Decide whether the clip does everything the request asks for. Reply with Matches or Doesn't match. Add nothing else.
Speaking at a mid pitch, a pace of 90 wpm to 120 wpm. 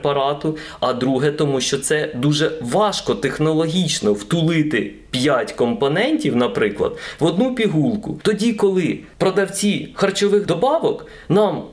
Matches